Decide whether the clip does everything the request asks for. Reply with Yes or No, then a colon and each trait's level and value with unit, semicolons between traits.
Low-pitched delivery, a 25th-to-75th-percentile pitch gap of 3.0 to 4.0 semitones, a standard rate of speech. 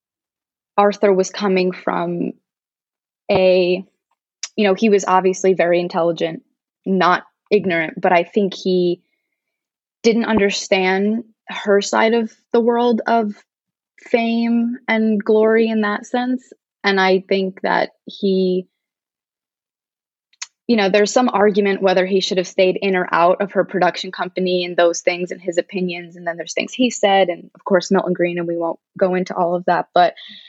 No: high, 190 Hz; average, 3.3 semitones; average, 155 wpm